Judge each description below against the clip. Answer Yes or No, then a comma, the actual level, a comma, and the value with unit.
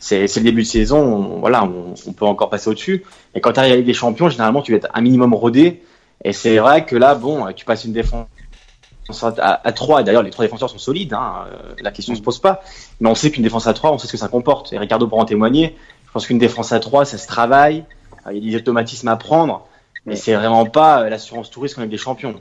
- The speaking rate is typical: No, fast, 260 wpm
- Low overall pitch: Yes, low, 115 Hz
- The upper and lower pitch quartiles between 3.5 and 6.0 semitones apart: Yes, average, 3.8 semitones